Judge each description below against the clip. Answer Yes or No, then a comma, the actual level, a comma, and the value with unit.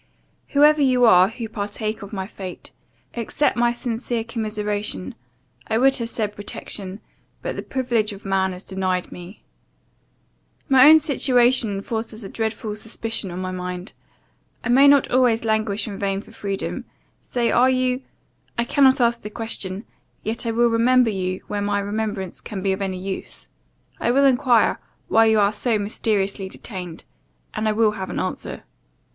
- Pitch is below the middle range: No, high, 220 Hz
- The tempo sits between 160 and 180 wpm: Yes, average, 165 wpm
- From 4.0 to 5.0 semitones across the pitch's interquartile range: No, average, 3.3 semitones